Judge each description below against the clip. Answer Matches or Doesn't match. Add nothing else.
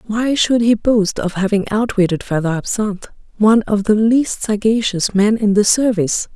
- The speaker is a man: Doesn't match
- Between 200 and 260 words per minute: Doesn't match